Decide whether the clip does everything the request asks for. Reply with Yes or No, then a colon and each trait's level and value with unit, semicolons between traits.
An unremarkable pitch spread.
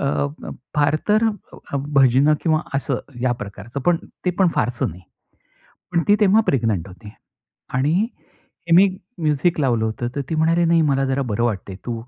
No: wide, 5.7 semitones